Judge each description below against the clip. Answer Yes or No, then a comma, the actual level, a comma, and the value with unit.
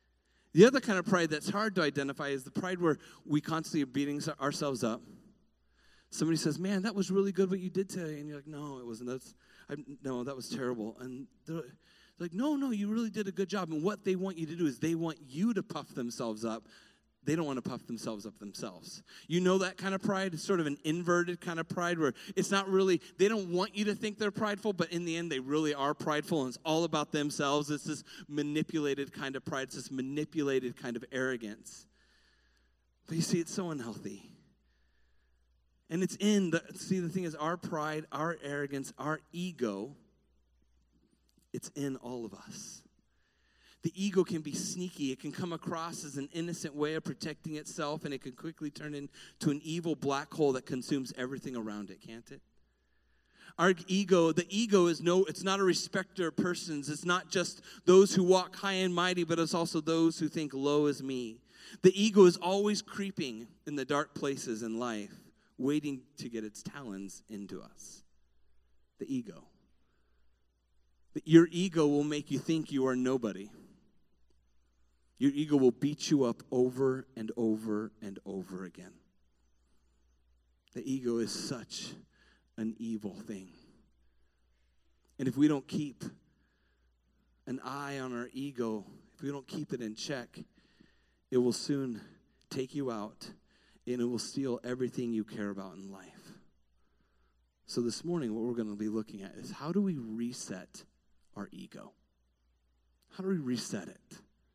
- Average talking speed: Yes, average, 185 wpm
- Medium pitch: Yes, medium, 145 Hz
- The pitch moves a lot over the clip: Yes, wide, 7.4 semitones